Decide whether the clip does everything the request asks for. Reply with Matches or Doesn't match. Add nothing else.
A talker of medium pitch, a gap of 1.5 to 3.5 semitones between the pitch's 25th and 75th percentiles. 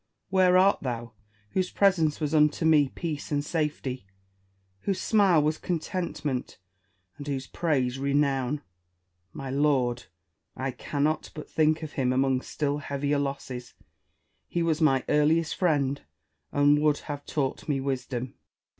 Matches